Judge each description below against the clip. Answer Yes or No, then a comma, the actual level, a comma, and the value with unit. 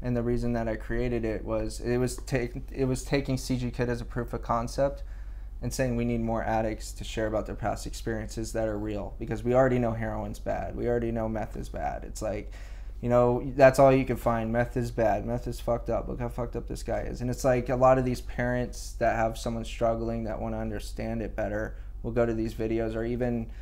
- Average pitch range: No, narrow, 1.8 semitones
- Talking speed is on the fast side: Yes, fast, 245 wpm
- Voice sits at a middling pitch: No, low, 115 Hz